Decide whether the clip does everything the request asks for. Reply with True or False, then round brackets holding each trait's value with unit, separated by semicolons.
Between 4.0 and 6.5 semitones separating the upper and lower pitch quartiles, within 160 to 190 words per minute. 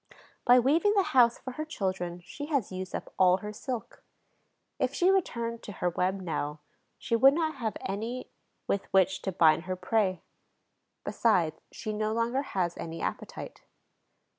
True (5.6 semitones; 165 wpm)